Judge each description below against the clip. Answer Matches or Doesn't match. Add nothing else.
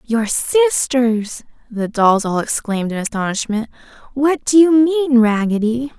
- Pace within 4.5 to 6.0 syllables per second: Doesn't match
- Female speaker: Matches